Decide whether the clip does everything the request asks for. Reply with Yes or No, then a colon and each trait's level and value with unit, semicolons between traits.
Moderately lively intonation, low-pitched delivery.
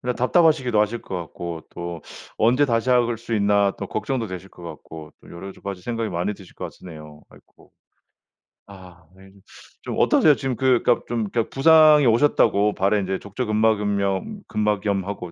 Yes: average, 4.1 semitones; low, 105 Hz